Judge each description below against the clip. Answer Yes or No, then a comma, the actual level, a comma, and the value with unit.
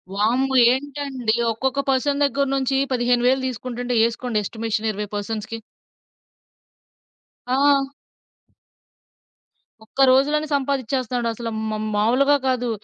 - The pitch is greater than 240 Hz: Yes, very high, 250 Hz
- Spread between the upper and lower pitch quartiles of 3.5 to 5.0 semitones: No, average, 2.9 semitones